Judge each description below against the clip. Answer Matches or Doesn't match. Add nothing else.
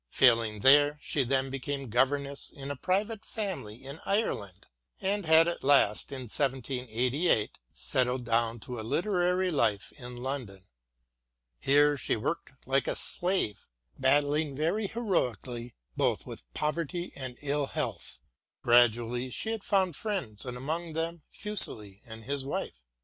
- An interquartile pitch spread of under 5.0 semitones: Doesn't match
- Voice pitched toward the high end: Doesn't match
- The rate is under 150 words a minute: Matches